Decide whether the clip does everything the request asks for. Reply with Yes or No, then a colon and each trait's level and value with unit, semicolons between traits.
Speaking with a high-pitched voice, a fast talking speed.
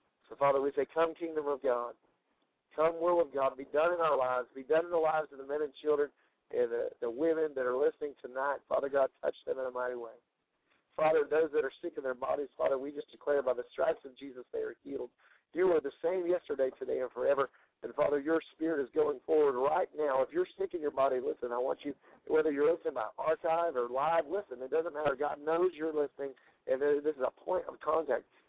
No: medium, 160 Hz; fast, 235 wpm